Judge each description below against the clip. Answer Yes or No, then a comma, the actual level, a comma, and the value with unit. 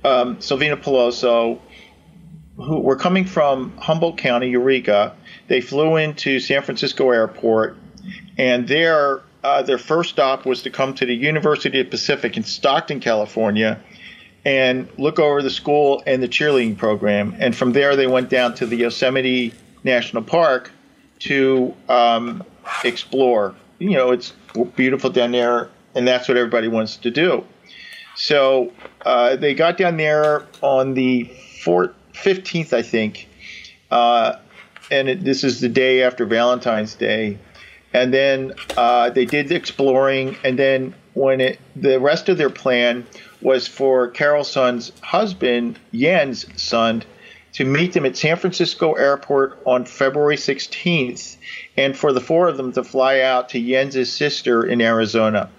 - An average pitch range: Yes, average, 3.2 semitones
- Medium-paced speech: Yes, average, 150 wpm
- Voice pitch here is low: Yes, low, 130 Hz